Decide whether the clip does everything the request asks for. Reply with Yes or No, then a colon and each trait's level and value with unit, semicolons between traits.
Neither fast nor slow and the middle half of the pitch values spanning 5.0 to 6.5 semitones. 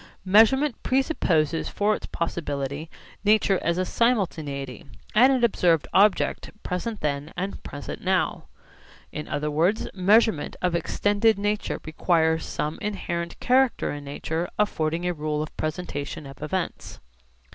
No: slow, 130 wpm; average, 5.3 semitones